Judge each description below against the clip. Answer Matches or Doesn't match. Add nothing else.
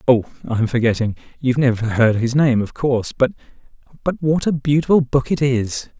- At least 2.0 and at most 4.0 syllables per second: Doesn't match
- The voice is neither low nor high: Doesn't match